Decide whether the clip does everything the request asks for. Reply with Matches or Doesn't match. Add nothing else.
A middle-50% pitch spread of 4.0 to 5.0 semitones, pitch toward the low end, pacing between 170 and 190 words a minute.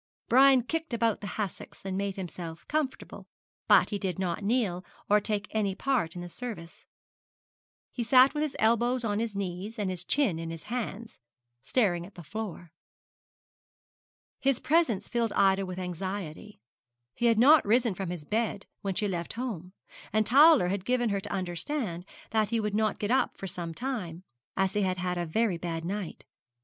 Doesn't match